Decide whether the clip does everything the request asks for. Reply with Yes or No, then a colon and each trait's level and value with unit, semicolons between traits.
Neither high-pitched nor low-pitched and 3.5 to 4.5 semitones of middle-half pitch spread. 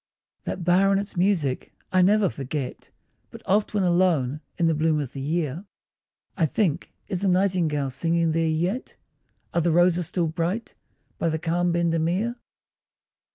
No: medium, 170 Hz; average, 2.8 semitones